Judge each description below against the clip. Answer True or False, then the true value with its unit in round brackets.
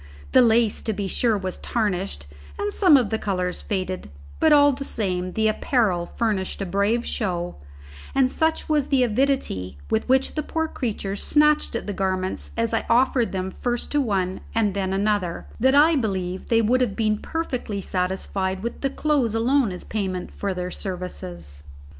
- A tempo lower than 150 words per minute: False (175 wpm)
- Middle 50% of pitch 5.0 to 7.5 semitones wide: True (5.3 semitones)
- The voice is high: True (215 Hz)